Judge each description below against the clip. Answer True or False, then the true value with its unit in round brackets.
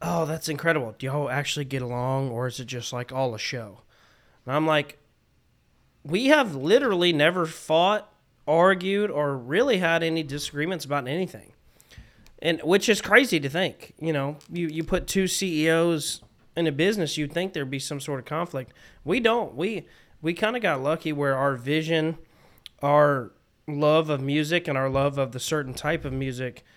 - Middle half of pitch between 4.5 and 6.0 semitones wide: False (3.5 semitones)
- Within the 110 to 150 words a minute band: False (175 wpm)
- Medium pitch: True (155 Hz)